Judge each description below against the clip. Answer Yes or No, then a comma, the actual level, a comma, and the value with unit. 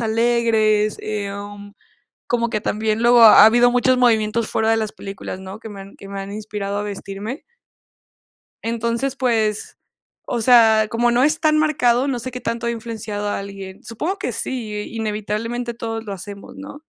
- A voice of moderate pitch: No, high, 225 Hz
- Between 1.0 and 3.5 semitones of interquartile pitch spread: Yes, narrow, 2.5 semitones